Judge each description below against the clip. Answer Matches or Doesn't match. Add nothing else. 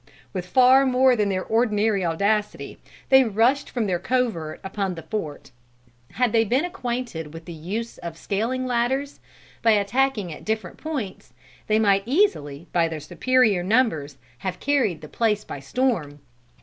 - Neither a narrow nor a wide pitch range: Doesn't match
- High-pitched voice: Matches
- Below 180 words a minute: Matches